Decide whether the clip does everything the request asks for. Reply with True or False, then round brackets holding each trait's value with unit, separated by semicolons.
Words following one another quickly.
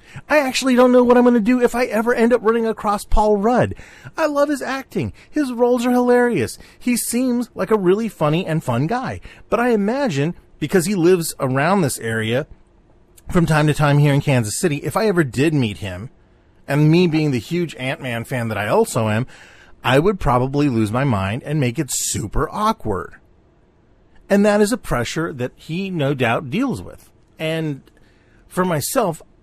False (195 wpm)